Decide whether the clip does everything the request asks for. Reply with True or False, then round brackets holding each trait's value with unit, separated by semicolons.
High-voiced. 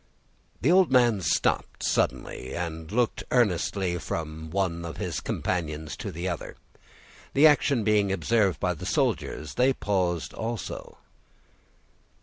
False (95 Hz)